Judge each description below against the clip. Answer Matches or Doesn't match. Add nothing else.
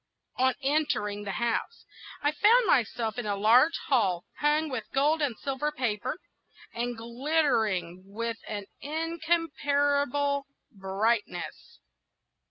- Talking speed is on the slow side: Matches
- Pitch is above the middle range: Matches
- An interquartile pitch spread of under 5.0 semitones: Doesn't match